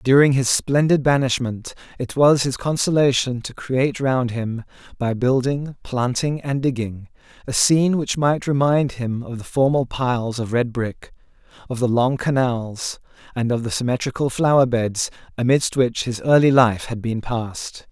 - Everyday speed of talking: Yes, average, 160 wpm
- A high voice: No, low, 125 Hz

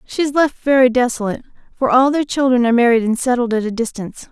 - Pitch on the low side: No, high, 245 Hz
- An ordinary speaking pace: No, fast, 225 wpm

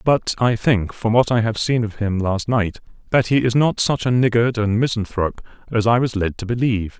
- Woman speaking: No, male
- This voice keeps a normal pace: No, fast, 230 wpm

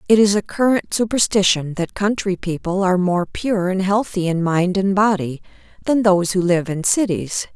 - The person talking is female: Yes, female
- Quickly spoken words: No, average, 185 wpm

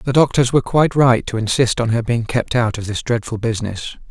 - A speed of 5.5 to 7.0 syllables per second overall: Yes, 6.0 syllables/s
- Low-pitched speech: Yes, low, 120 Hz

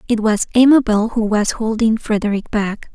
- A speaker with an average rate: Yes, average, 165 wpm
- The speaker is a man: No, female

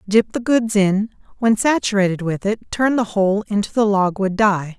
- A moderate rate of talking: Yes, average, 175 wpm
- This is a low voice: No, high, 205 Hz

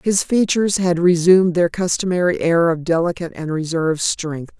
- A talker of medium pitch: Yes, medium, 175 Hz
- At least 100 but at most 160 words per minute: Yes, average, 155 wpm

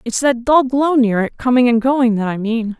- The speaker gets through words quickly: Yes, fast, 255 wpm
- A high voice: Yes, high, 245 Hz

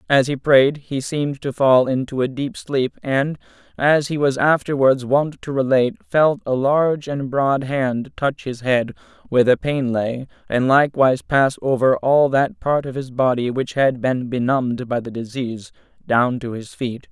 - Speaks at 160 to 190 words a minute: Yes, average, 185 wpm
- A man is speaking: Yes, male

